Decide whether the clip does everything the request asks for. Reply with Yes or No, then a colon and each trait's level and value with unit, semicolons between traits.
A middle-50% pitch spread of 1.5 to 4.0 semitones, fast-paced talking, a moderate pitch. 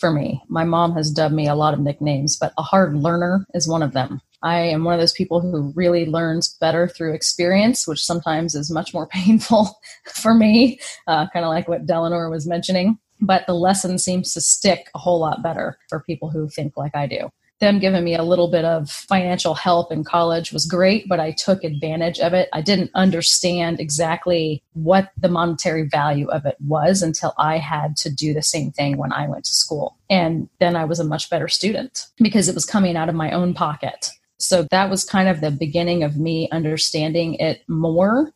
Yes: narrow, 2.5 semitones; fast, 215 wpm; medium, 170 Hz